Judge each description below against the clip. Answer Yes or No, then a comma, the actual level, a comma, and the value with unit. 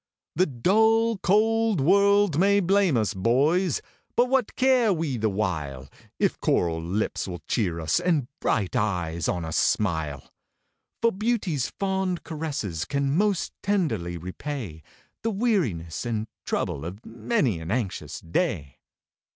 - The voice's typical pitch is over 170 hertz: No, low, 135 Hz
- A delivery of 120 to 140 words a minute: Yes, slow, 135 wpm